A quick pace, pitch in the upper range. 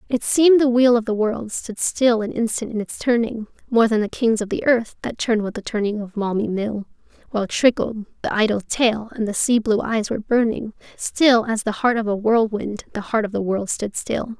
Yes: fast, 230 wpm; high, 225 Hz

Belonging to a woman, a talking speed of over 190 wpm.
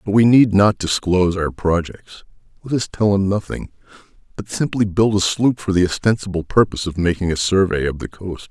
No: male; average, 200 wpm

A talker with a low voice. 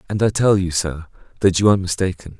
Yes: very low, 95 Hz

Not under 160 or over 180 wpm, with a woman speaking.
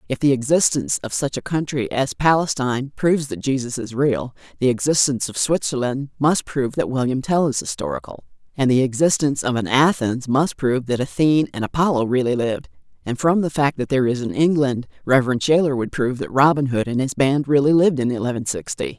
No: average, 200 wpm; female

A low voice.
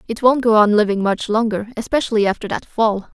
No: high, 220 Hz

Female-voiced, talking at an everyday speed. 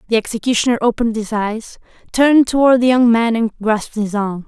Yes: female; average, 190 wpm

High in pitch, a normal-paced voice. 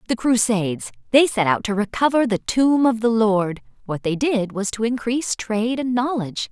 Yes: high, 225 Hz; average, 175 wpm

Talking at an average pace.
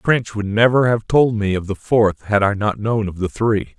No: fast, 255 wpm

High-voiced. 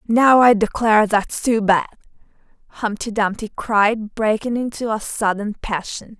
Yes: high, 215 Hz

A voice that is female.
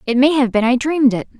Yes: female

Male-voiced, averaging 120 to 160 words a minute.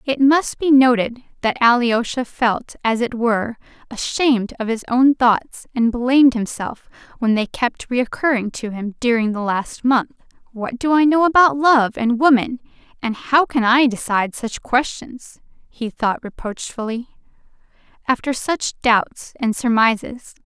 No: female; average, 150 wpm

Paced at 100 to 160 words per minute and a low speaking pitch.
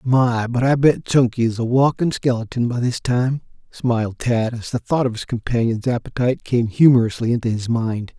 No: average, 190 wpm; low, 120 Hz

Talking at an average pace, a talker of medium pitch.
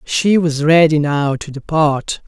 Yes: average, 160 wpm; medium, 155 Hz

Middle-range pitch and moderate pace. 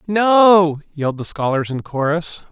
Yes: medium, 165 Hz; average, 145 wpm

